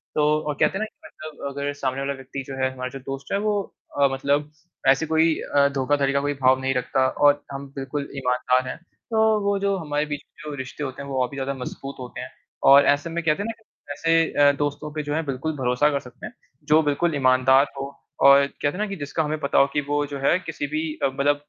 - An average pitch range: No, narrow, 2.2 semitones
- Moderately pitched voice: Yes, medium, 145 Hz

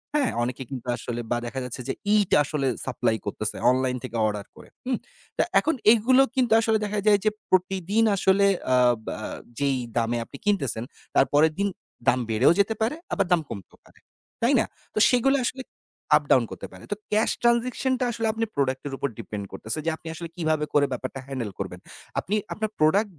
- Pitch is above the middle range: No, medium, 160 Hz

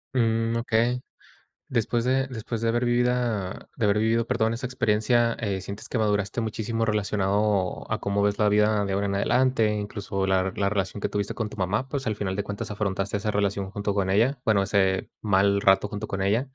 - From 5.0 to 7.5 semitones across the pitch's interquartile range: No, narrow, 2.5 semitones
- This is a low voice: Yes, low, 105 Hz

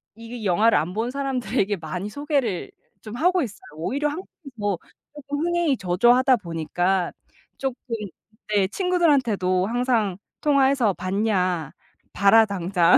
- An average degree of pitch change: No, wide, 6.6 semitones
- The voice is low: No, high, 220 Hz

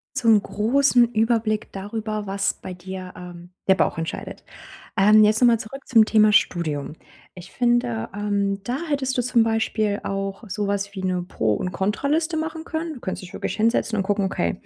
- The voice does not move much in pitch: No, average, 3.7 semitones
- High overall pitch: Yes, high, 210 Hz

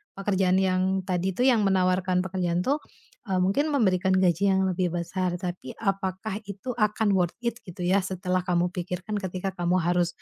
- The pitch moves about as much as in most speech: No, narrow, 1.5 semitones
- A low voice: No, medium, 185 Hz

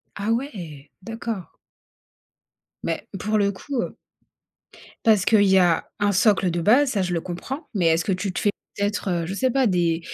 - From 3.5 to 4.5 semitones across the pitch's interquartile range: Yes, average, 4.0 semitones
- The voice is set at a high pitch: Yes, high, 200 Hz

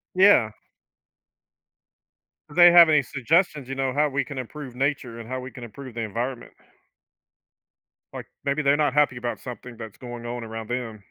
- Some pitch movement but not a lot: Yes, average, 3.5 semitones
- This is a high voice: No, low, 130 Hz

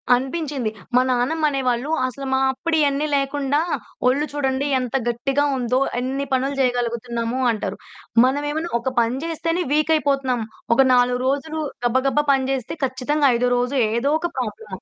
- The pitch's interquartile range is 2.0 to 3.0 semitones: Yes, average, 2.7 semitones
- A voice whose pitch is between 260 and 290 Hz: Yes, very high, 265 Hz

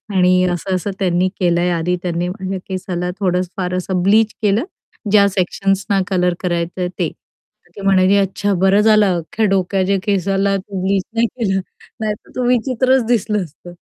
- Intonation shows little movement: Yes, narrow, 2.1 semitones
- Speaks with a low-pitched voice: No, high, 190 Hz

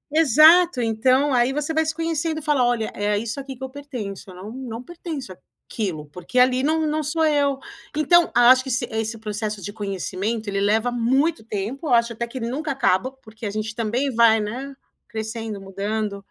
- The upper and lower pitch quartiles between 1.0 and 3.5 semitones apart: No, average, 4.6 semitones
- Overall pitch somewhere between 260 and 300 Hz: No, high, 240 Hz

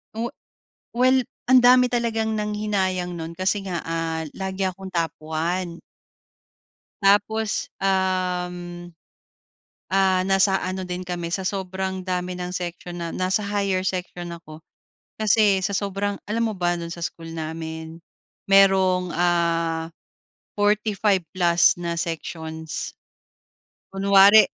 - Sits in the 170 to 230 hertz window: Yes, medium, 185 Hz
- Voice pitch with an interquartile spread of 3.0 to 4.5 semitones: No, narrow, 2.5 semitones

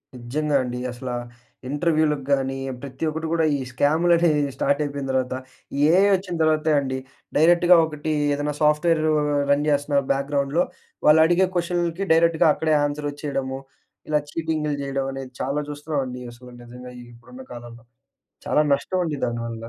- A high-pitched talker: No, medium, 145 Hz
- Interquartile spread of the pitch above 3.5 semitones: No, average, 3.1 semitones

